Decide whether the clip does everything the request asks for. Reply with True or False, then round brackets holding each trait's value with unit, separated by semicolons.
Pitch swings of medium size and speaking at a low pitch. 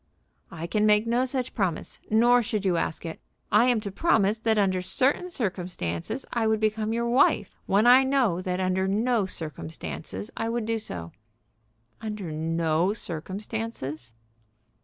False (4.5 semitones; 210 Hz)